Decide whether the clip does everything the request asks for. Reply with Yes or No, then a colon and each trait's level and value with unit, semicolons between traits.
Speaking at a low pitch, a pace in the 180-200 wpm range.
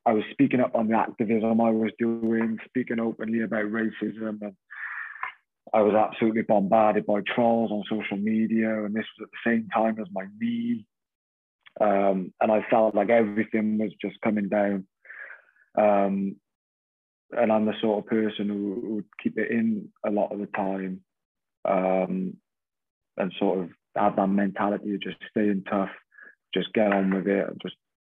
No: low, 110 Hz; average, 170 wpm